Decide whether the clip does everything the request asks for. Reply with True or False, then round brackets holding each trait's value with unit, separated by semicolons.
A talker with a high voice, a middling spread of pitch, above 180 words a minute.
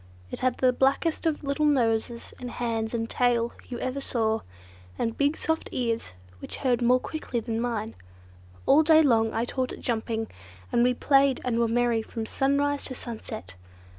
False (245 Hz; 3.1 semitones; 175 wpm)